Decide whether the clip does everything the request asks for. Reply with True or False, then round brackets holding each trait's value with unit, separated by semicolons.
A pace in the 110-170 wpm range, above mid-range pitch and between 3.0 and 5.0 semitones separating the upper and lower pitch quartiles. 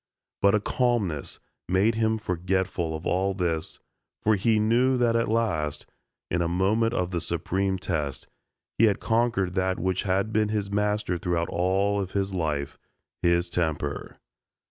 False (155 wpm; 95 Hz; 3.6 semitones)